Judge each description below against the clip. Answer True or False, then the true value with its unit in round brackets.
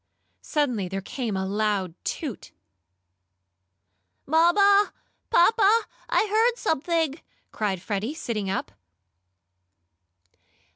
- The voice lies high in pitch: True (270 Hz)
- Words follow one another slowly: True (85 wpm)